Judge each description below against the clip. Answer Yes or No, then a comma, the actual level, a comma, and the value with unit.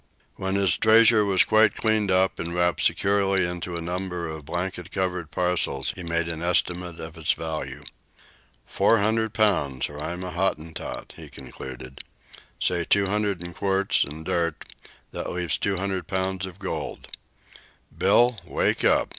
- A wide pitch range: No, average, 2.8 semitones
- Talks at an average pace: Yes, average, 155 wpm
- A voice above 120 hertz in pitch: No, very low, 90 Hz